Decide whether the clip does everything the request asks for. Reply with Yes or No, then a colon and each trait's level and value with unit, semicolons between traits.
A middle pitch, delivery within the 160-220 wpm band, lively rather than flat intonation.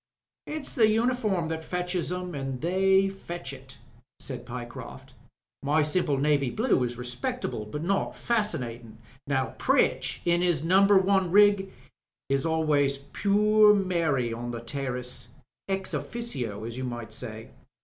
No: medium, 160 Hz; average, 140 wpm; wide, 7.1 semitones